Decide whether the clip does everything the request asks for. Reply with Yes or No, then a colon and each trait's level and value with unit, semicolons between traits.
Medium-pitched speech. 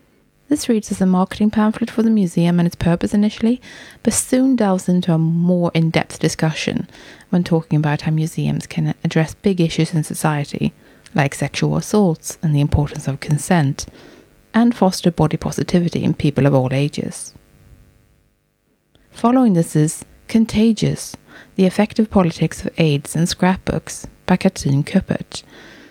Yes: medium, 175 Hz